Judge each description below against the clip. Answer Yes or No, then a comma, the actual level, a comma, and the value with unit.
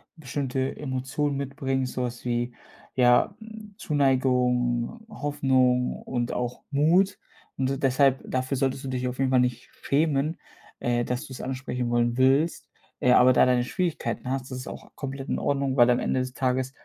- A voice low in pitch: Yes, low, 130 Hz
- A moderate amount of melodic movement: No, narrow, 1.9 semitones